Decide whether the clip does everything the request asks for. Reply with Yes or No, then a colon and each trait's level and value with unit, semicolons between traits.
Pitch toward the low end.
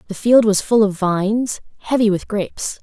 No: high, 210 Hz